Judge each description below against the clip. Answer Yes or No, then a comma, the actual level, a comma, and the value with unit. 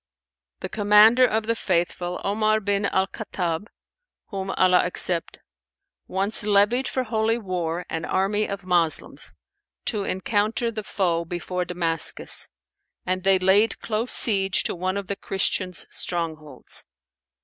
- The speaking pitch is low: No, high, 195 Hz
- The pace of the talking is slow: Yes, slow, 130 wpm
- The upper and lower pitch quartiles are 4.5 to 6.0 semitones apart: No, average, 3.1 semitones